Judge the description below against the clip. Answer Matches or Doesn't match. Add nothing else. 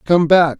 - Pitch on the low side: Doesn't match